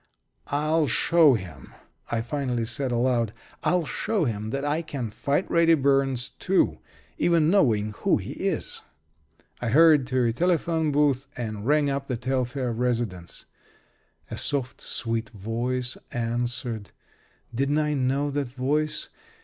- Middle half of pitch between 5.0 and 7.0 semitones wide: No, average, 3.9 semitones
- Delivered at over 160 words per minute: No, slow, 135 wpm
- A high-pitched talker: No, low, 130 Hz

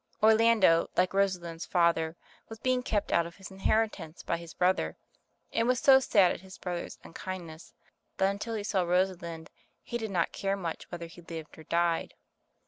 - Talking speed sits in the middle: Yes, average, 180 wpm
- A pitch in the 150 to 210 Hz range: Yes, medium, 185 Hz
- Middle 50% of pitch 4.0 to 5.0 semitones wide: No, average, 3.4 semitones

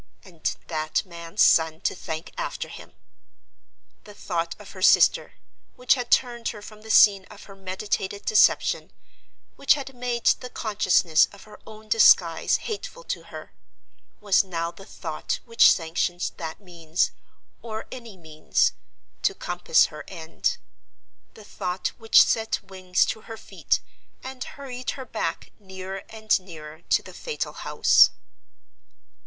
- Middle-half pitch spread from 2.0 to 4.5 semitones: No, average, 4.9 semitones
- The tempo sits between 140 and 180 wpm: Yes, average, 145 wpm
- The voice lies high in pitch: Yes, high, 195 Hz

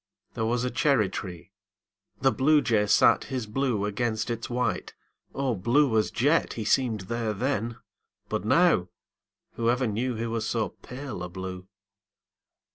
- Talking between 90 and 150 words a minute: Yes, average, 145 wpm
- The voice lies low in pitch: Yes, low, 115 Hz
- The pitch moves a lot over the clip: No, average, 3.4 semitones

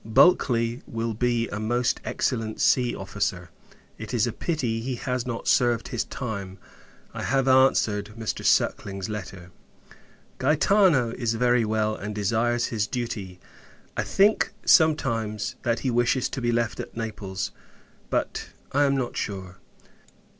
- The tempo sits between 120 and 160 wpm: Yes, average, 140 wpm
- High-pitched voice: No, low, 115 Hz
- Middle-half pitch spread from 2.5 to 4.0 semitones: Yes, average, 2.9 semitones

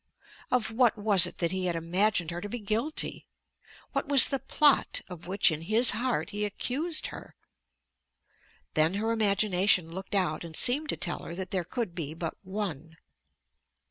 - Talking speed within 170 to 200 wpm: Yes, average, 175 wpm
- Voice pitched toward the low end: No, high, 195 Hz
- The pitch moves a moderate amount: Yes, average, 4.7 semitones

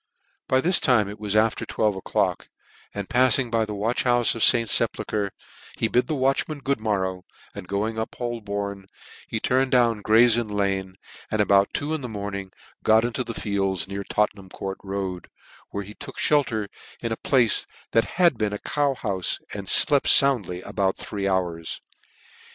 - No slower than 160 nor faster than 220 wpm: Yes, average, 175 wpm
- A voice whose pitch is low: Yes, low, 110 Hz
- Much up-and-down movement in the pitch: No, average, 3.6 semitones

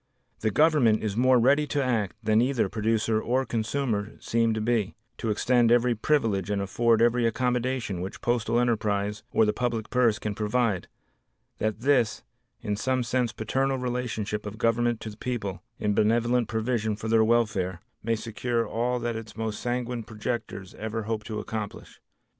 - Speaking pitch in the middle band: No, low, 115 Hz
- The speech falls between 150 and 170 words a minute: Yes, average, 165 wpm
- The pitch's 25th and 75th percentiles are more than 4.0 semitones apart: No, narrow, 2.4 semitones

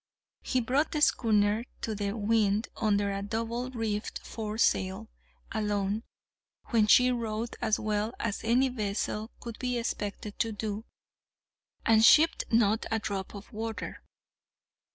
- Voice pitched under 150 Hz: No, high, 220 Hz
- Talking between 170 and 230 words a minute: No, slow, 135 wpm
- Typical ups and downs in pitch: No, narrow, 1.9 semitones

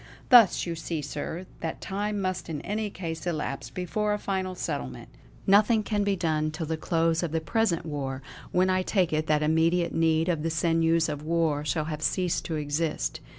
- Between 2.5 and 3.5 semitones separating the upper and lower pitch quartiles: Yes, average, 3.2 semitones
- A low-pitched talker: No, medium, 165 Hz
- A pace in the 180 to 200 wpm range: Yes, average, 195 wpm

